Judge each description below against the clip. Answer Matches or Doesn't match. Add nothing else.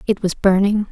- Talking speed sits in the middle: Matches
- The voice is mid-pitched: Doesn't match